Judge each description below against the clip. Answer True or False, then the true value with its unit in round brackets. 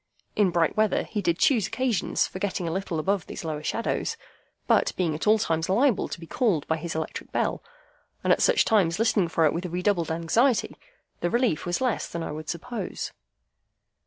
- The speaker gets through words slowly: False (195 wpm)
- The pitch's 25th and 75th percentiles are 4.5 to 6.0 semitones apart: True (5.0 semitones)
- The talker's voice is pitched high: False (180 Hz)